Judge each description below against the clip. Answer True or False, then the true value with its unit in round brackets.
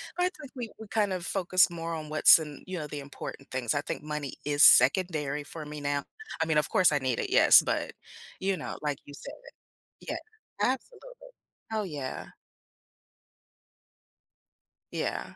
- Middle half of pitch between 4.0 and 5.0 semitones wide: True (4.6 semitones)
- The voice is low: False (155 Hz)